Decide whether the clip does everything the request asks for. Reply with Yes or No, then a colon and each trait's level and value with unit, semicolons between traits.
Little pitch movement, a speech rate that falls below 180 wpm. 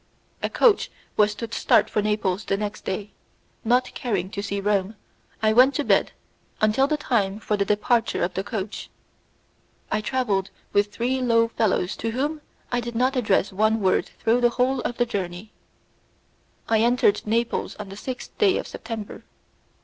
No: average, 3.3 semitones; average, 170 wpm